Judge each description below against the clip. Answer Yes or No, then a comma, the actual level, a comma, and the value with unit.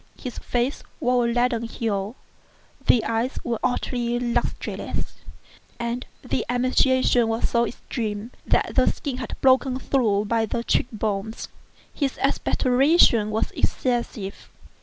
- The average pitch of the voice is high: Yes, high, 240 Hz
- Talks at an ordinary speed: No, slow, 130 wpm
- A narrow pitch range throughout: Yes, narrow, 2.0 semitones